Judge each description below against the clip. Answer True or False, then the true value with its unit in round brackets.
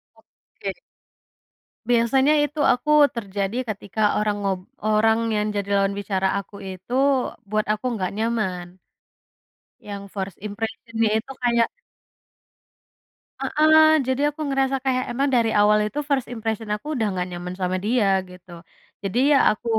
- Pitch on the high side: True (215 Hz)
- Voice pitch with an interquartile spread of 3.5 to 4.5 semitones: True (3.9 semitones)